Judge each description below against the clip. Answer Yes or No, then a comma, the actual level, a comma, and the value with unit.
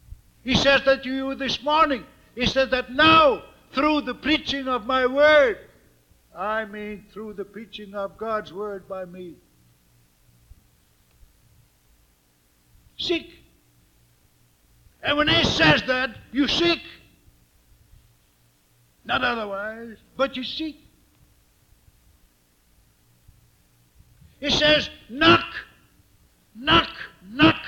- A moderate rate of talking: No, slow, 100 wpm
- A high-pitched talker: Yes, high, 215 Hz